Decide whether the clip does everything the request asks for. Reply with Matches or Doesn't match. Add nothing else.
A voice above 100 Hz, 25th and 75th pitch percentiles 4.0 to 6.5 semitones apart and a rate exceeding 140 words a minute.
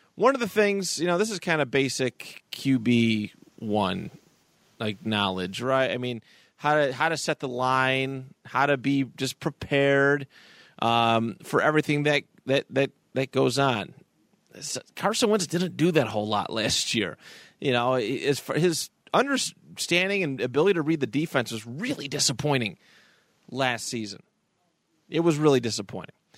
Matches